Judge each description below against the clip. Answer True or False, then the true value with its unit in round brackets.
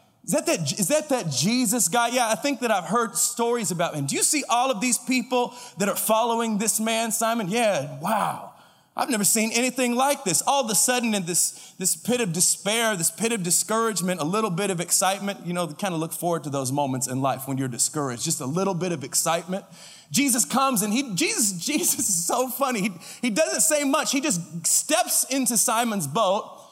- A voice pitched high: True (220 Hz)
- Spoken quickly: True (220 wpm)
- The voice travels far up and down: True (6.0 semitones)